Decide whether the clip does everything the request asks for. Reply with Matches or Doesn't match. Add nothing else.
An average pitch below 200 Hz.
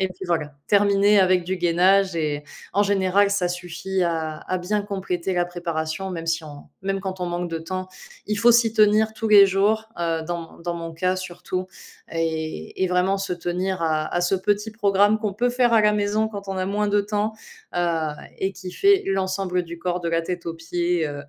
Matches